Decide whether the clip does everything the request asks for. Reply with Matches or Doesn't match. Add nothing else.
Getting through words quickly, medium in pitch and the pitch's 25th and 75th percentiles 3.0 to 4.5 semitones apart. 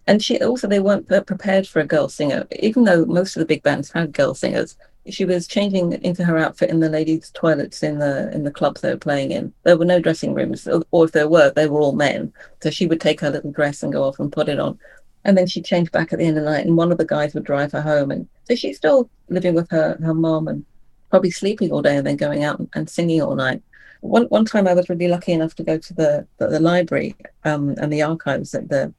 Matches